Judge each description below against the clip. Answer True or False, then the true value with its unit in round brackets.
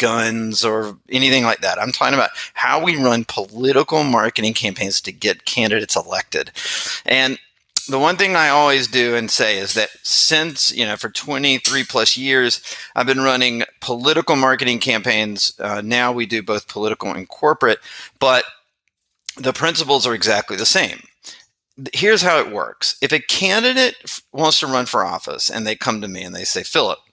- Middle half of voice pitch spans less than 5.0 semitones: True (3.7 semitones)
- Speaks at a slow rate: False (175 wpm)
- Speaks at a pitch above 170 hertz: False (125 Hz)